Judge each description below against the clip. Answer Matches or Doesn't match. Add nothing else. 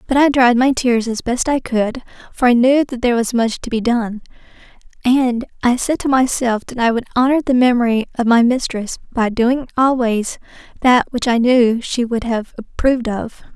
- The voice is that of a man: Doesn't match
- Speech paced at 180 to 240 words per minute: Matches